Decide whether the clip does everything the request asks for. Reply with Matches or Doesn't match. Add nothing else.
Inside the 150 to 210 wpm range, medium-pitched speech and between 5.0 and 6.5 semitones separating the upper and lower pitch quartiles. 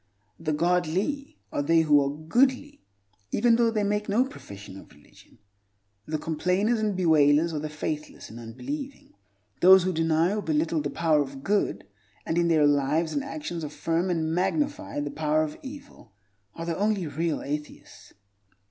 Matches